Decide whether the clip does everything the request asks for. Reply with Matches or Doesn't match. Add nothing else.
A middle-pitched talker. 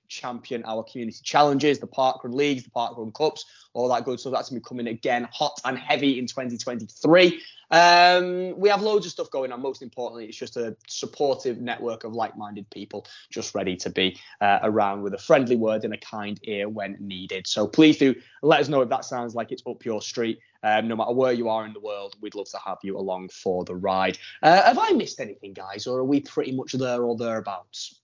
Doesn't match